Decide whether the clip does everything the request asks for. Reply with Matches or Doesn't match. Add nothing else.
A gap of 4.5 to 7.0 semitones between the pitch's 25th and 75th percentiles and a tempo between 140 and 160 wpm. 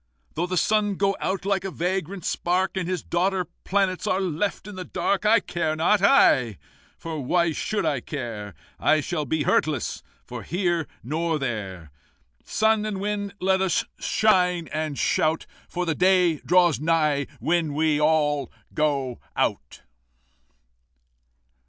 Doesn't match